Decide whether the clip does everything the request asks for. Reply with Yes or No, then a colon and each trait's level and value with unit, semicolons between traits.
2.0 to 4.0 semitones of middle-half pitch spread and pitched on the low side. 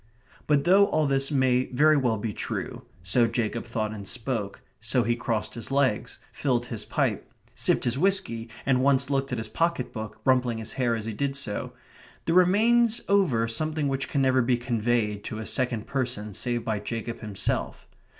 Yes: average, 3.7 semitones; low, 125 Hz